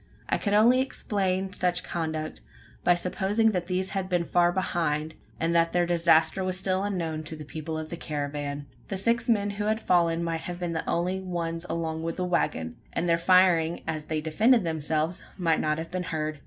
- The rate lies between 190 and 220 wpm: Yes, average, 200 wpm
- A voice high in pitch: No, medium, 170 Hz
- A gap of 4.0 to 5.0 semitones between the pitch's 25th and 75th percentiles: No, average, 2.7 semitones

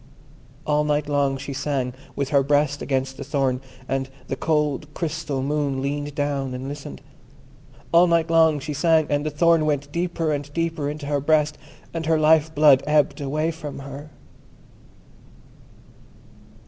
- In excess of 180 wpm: No, average, 155 wpm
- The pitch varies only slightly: Yes, narrow, 1.9 semitones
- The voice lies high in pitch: No, medium, 145 Hz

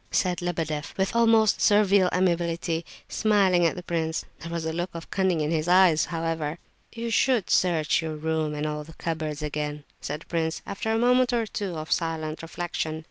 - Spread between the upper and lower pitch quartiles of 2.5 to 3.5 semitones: Yes, average, 3.2 semitones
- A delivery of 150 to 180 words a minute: No, average, 190 wpm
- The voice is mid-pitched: Yes, medium, 165 Hz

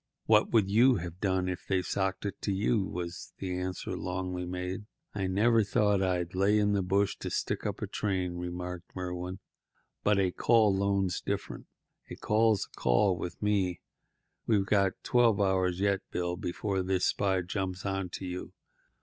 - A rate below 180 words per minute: Yes, average, 170 wpm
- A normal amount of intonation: No, narrow, 1.9 semitones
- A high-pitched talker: No, very low, 95 Hz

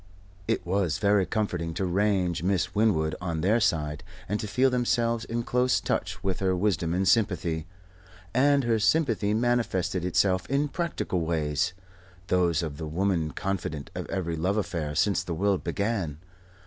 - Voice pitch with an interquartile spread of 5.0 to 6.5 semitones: No, average, 4.3 semitones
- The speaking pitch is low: Yes, very low, 95 Hz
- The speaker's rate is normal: Yes, average, 160 wpm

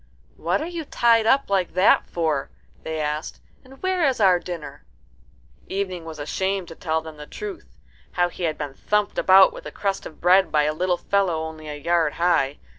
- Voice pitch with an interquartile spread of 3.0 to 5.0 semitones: Yes, average, 4.0 semitones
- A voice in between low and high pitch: Yes, medium, 175 Hz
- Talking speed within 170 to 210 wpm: Yes, average, 195 wpm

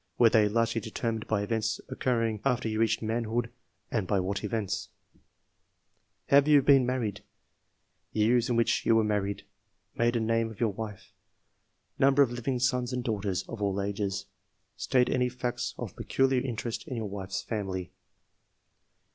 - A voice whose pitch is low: Yes, low, 115 Hz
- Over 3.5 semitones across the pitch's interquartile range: No, average, 2.9 semitones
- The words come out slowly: No, average, 155 wpm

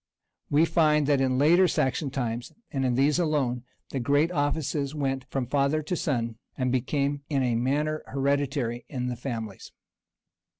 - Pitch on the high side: No, medium, 140 Hz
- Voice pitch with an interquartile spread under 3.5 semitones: Yes, average, 2.9 semitones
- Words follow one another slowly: No, average, 175 wpm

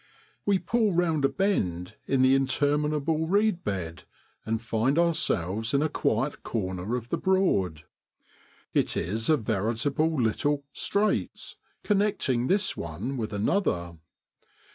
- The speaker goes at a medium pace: No, slow, 130 wpm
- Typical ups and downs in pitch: No, wide, 7.5 semitones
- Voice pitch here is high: No, low, 135 Hz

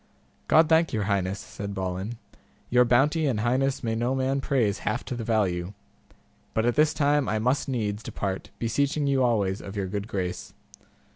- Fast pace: No, average, 180 wpm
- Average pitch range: Yes, average, 4.9 semitones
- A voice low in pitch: Yes, low, 115 Hz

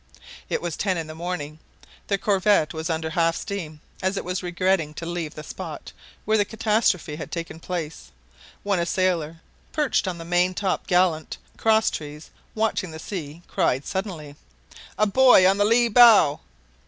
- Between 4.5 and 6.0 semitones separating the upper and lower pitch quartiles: No, average, 4.0 semitones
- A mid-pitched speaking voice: Yes, medium, 180 Hz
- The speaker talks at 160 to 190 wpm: Yes, average, 165 wpm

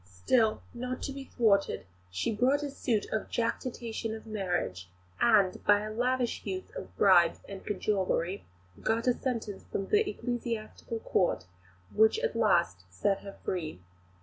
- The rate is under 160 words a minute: Yes, average, 150 wpm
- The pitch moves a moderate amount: Yes, average, 4.1 semitones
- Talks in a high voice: Yes, high, 215 Hz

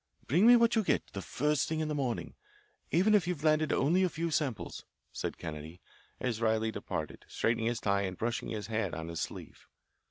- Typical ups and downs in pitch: No, wide, 6.9 semitones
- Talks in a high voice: No, low, 125 Hz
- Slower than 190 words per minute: No, average, 200 wpm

